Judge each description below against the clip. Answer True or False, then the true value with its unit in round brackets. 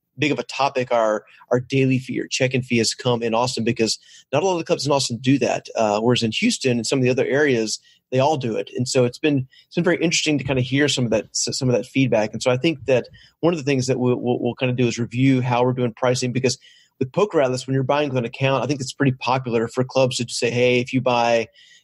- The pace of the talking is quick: True (285 wpm)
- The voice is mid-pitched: False (125 Hz)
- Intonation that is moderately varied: False (2.1 semitones)